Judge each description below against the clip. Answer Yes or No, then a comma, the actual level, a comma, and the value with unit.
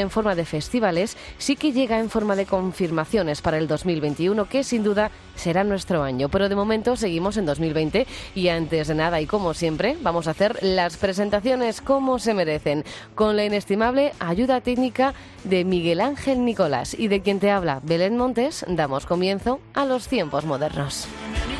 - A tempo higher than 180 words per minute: No, average, 175 wpm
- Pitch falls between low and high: No, high, 195 Hz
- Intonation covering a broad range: Yes, wide, 5.7 semitones